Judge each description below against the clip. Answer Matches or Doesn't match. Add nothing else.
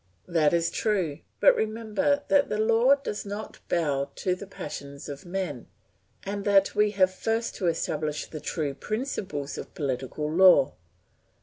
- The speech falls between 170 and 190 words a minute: Doesn't match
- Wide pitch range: Matches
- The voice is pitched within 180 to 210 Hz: Matches